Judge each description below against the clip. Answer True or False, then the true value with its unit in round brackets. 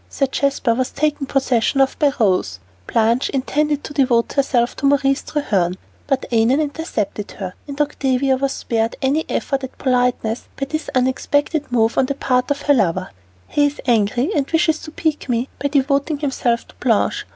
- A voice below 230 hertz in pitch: False (270 Hz)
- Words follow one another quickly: False (175 wpm)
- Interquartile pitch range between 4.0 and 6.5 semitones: False (3.4 semitones)